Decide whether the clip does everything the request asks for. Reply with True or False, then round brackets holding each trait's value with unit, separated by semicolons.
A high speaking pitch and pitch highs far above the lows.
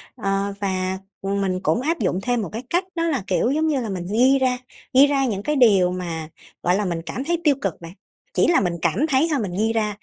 True (215 Hz; 6.3 semitones)